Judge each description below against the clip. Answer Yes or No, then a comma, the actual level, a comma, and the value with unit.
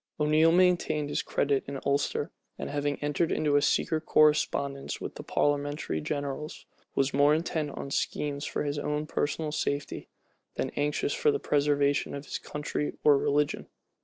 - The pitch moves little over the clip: Yes, narrow, 1.3 semitones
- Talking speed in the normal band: Yes, average, 160 wpm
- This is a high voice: No, medium, 145 Hz